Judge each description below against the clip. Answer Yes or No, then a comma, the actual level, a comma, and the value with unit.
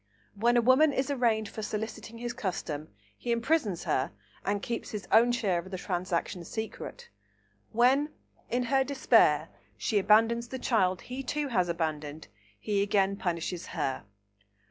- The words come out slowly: No, average, 150 wpm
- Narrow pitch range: No, average, 4.7 semitones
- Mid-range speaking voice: No, high, 220 Hz